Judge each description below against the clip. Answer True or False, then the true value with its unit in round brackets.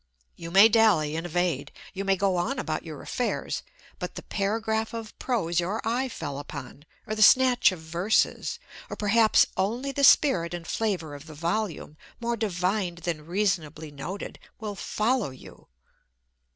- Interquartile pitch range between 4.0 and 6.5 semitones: True (4.8 semitones)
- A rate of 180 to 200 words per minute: False (160 wpm)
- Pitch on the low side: False (195 Hz)